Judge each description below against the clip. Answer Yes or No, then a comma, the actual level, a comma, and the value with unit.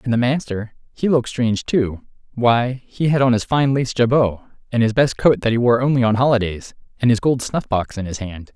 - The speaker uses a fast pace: Yes, fast, 225 wpm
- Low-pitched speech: Yes, low, 120 Hz